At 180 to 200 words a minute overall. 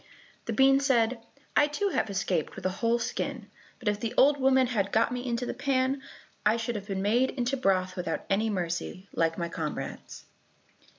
Yes: average, 190 wpm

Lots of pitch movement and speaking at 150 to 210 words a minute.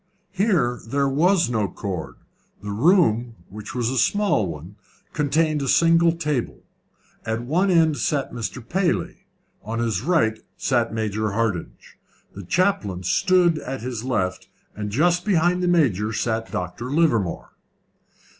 No: wide, 7.5 semitones; slow, 135 wpm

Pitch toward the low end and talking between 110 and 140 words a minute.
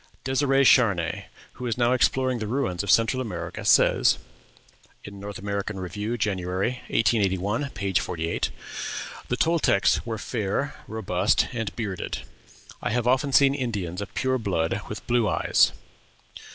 Yes: low, 110 Hz; slow, 135 wpm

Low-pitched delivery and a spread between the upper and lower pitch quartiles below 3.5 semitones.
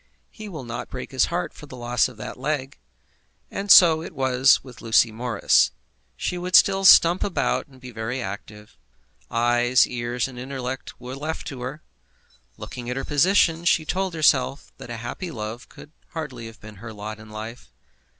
No: low, 130 Hz; average, 4.8 semitones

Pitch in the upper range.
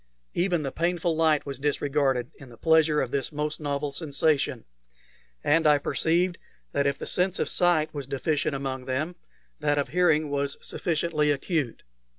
No: medium, 150 Hz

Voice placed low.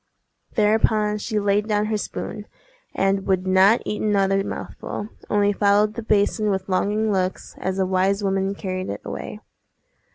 No: high, 200 Hz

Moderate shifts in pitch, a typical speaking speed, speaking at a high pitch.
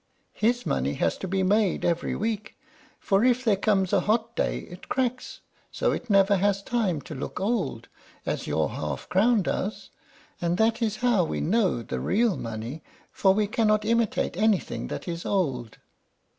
Yes: average, 4.1 semitones; average, 170 wpm; high, 205 Hz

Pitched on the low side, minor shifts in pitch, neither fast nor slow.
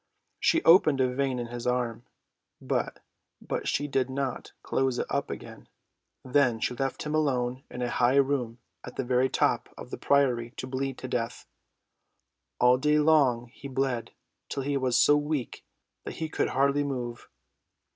Yes: low, 130 Hz; narrow, 2.3 semitones; average, 165 wpm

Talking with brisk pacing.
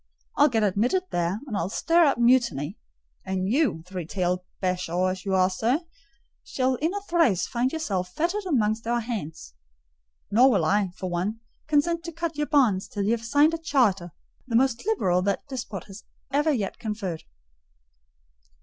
No: average, 165 wpm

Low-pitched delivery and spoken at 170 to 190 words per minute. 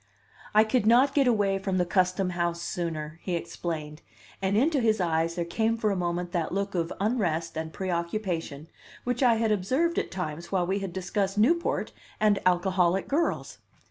No: high, 190 Hz; average, 175 wpm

